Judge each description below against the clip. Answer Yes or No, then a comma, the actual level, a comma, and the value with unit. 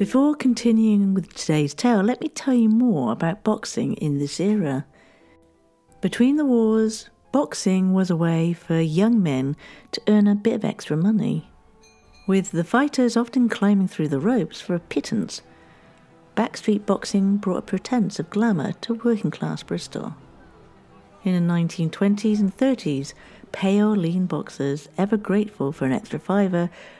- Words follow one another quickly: No, average, 150 wpm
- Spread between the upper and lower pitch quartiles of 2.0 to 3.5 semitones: No, average, 5.3 semitones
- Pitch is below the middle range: No, high, 200 Hz